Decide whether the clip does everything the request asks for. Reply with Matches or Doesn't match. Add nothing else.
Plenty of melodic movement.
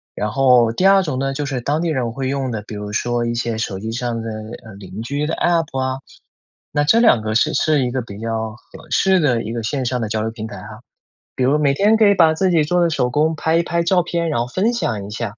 Matches